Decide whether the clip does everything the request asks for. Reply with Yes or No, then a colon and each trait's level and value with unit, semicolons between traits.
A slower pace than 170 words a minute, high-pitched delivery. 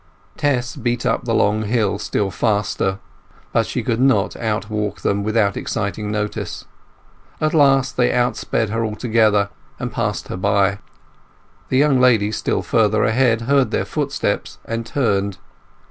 No: average, 145 wpm; low, 110 Hz